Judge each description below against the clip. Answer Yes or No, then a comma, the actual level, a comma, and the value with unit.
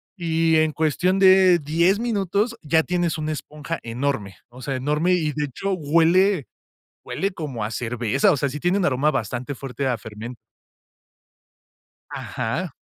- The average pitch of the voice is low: No, medium, 155 Hz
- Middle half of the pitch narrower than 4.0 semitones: No, wide, 5.4 semitones